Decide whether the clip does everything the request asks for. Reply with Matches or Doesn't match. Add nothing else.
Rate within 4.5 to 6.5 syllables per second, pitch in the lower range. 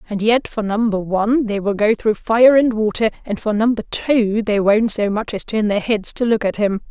Doesn't match